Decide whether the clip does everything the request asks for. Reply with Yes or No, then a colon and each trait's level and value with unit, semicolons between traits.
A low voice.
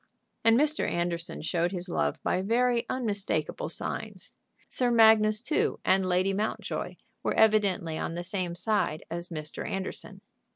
No: high, 195 Hz